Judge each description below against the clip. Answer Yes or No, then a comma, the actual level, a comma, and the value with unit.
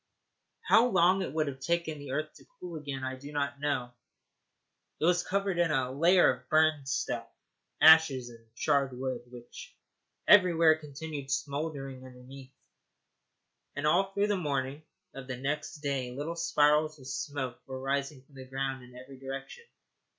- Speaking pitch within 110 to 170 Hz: Yes, medium, 140 Hz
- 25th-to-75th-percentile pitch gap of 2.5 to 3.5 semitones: Yes, average, 3.1 semitones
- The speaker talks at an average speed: Yes, average, 160 wpm